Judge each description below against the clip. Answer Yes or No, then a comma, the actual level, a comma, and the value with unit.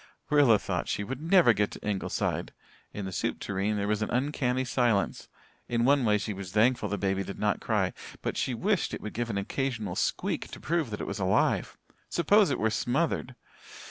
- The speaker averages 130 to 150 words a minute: No, fast, 205 wpm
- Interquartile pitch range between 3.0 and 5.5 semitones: Yes, average, 4.6 semitones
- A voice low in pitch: Yes, low, 115 Hz